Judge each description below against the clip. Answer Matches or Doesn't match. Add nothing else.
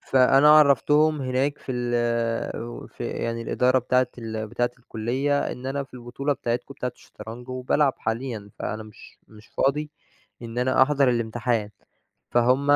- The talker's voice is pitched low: Matches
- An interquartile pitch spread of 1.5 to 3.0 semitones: Matches